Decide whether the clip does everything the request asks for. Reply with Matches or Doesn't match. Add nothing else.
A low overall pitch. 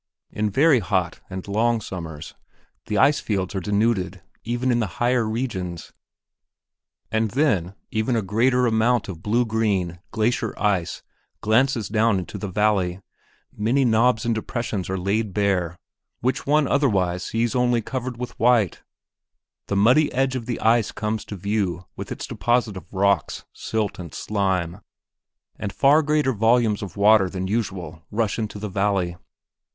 Matches